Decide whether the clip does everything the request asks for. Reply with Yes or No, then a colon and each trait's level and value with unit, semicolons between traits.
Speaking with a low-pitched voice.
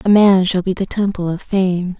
No: high, 190 Hz